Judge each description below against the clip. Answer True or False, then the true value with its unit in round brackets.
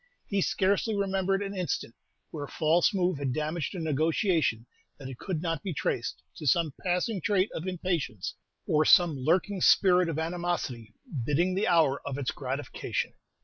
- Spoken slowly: False (165 wpm)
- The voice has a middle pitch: True (170 Hz)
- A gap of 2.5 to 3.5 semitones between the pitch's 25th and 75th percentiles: False (4.4 semitones)